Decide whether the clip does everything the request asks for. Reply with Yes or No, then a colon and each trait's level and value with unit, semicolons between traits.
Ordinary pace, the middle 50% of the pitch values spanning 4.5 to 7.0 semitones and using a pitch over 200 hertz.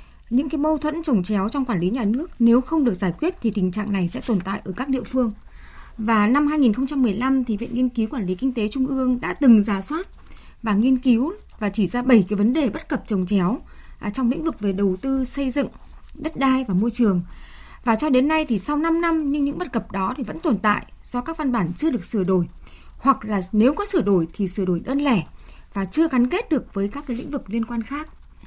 No: fast, 255 wpm; average, 5.2 semitones; high, 245 Hz